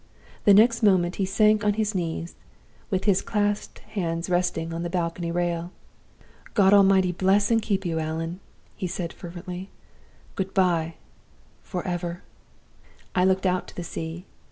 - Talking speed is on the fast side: No, average, 150 wpm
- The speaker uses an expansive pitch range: No, narrow, 2.5 semitones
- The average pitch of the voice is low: No, medium, 180 Hz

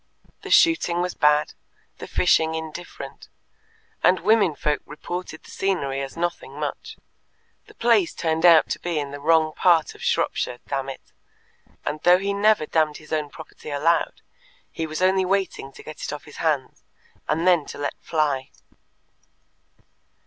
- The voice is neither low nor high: Yes, medium, 160 Hz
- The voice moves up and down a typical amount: Yes, average, 3.2 semitones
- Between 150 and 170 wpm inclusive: Yes, average, 160 wpm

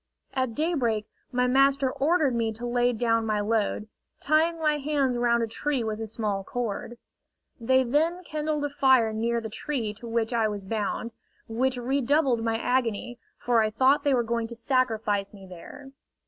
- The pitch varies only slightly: No, average, 3.5 semitones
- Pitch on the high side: Yes, high, 240 Hz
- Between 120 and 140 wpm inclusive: No, average, 175 wpm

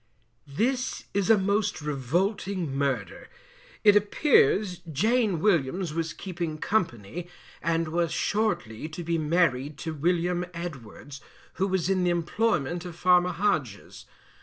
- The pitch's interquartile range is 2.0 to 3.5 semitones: No, average, 4.2 semitones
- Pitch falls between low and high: Yes, medium, 175 Hz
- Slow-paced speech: Yes, slow, 125 wpm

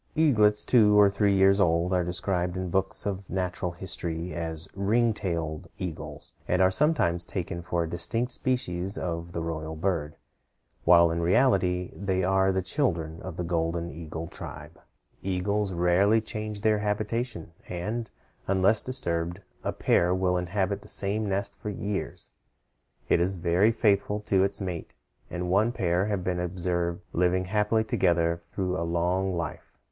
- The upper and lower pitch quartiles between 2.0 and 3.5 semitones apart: Yes, average, 2.9 semitones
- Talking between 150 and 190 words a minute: Yes, average, 155 wpm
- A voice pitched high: No, very low, 95 Hz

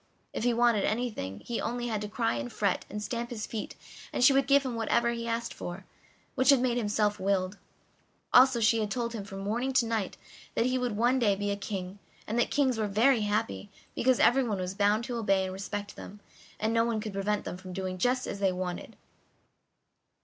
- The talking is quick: Yes, fast, 220 wpm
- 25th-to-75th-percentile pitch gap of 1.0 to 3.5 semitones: Yes, average, 3.1 semitones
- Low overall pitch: No, high, 220 Hz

